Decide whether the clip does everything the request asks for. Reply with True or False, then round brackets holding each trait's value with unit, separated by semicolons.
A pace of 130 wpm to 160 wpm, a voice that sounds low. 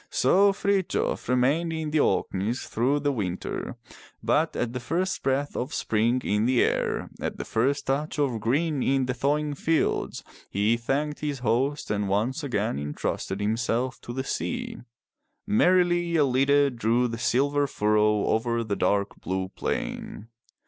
True (155 wpm; 130 Hz)